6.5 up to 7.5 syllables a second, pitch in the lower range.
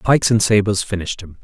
Yes: 6.6 syllables/s; low, 100 Hz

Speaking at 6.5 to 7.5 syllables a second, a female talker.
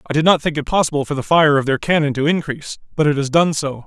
No: 6.7 syllables/s; male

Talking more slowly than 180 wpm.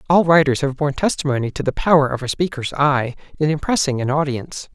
No: average, 200 wpm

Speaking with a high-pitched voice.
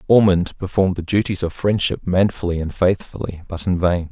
No: very low, 90 Hz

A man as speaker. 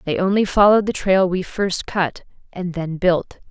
No: female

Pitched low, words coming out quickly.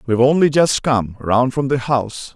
No: low, 130 Hz; average, 180 wpm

